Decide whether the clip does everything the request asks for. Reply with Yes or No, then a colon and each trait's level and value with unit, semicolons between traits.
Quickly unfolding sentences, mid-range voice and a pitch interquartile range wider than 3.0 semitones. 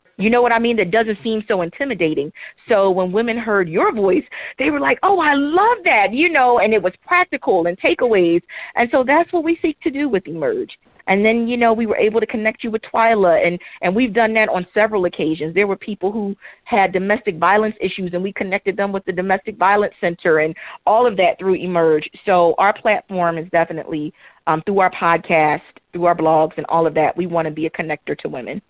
No: fast, 225 wpm; high, 200 Hz; average, 4.9 semitones